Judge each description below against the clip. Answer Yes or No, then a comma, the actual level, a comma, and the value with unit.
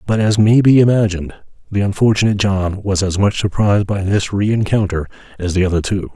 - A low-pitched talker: Yes, low, 100 Hz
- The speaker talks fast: No, average, 185 wpm